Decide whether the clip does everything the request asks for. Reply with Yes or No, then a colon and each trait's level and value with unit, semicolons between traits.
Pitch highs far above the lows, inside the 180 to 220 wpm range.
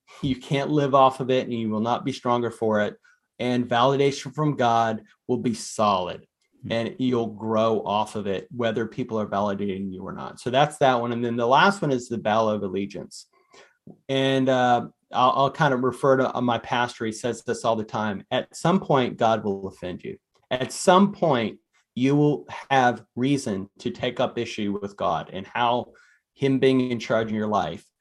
No: average, 3.2 semitones; average, 200 wpm